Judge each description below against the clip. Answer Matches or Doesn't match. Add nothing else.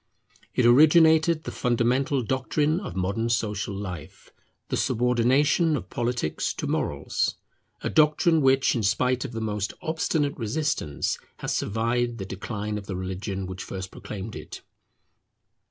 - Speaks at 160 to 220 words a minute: Doesn't match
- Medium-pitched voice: Doesn't match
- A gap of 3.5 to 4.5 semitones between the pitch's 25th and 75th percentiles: Doesn't match